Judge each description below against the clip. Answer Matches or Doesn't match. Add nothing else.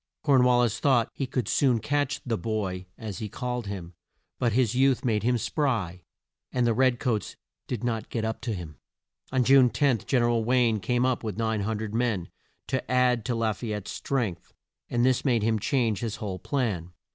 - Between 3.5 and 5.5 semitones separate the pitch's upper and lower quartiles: Doesn't match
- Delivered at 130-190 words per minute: Doesn't match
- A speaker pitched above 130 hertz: Doesn't match